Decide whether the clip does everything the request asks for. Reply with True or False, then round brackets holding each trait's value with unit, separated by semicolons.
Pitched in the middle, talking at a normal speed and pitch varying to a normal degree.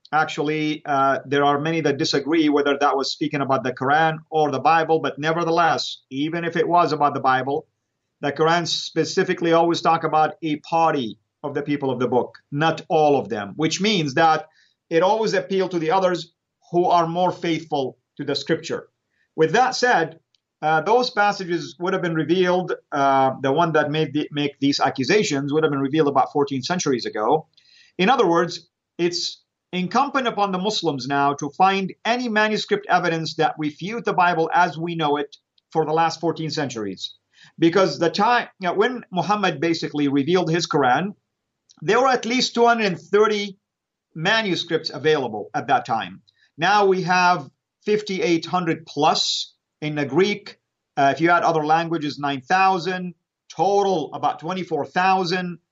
True (165 Hz; 165 wpm; 3.9 semitones)